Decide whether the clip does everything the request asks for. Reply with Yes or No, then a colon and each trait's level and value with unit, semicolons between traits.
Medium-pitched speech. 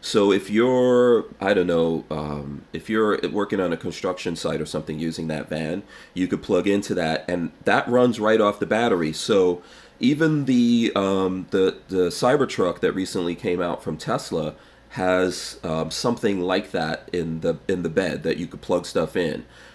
No: very low, 90 Hz